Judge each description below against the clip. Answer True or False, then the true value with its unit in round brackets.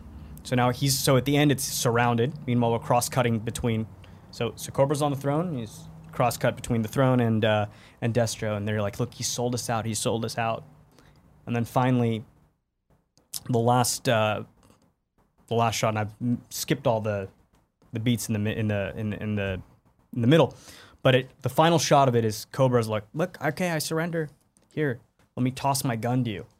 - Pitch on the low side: True (120 Hz)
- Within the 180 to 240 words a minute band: True (200 wpm)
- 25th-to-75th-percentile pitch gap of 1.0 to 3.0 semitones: False (3.4 semitones)